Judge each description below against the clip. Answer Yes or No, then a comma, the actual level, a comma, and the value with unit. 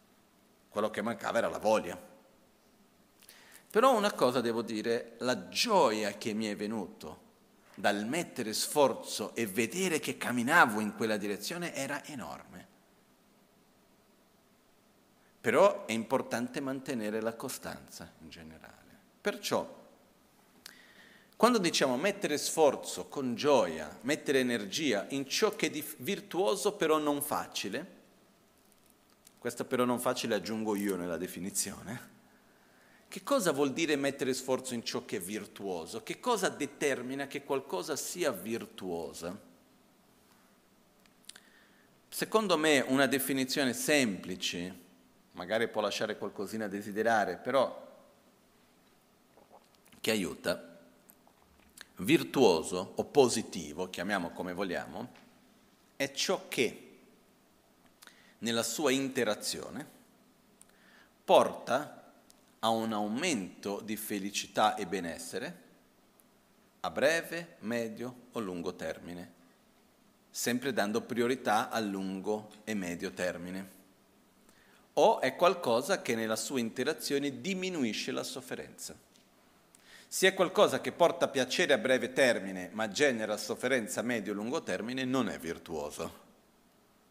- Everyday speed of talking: No, slow, 110 wpm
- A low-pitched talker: Yes, low, 125 Hz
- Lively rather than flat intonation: Yes, wide, 6.3 semitones